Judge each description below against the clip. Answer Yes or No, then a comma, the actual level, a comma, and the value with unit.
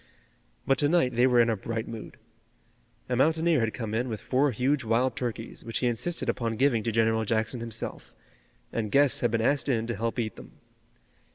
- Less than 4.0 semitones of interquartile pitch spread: Yes, narrow, 2.6 semitones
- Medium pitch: No, low, 120 Hz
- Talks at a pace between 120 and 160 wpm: No, average, 200 wpm